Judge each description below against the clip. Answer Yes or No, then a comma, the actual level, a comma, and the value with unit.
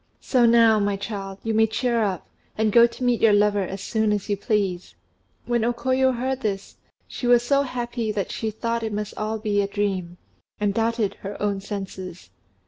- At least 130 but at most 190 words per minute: No, average, 200 wpm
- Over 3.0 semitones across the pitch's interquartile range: No, average, 2.7 semitones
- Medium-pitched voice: No, high, 215 Hz